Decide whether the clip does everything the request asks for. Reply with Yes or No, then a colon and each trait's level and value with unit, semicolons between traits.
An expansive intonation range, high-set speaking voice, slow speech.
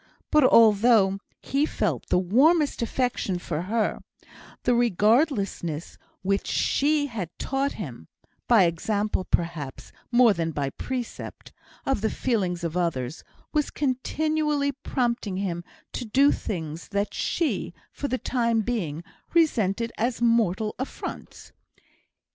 Yes: wide, 6.3 semitones; high, 220 Hz; slow, 120 wpm